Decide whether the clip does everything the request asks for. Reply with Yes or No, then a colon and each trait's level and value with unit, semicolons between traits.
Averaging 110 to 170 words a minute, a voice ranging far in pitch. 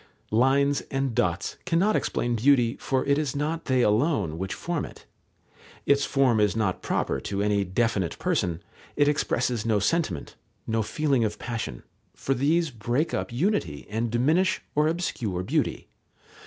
Yes: average, 155 wpm; wide, 5.7 semitones